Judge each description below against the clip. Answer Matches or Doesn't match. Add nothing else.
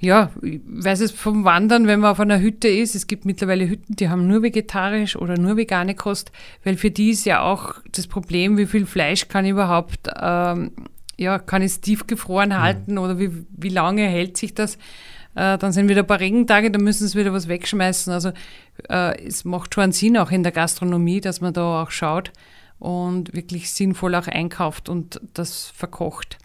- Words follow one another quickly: Matches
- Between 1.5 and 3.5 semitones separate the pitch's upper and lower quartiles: Matches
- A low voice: Doesn't match